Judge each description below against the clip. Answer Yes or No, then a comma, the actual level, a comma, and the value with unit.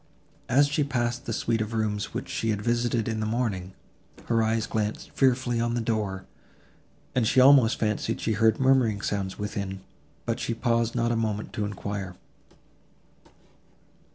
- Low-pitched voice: Yes, low, 115 Hz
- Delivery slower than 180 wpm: Yes, average, 160 wpm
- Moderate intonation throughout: No, narrow, 2.2 semitones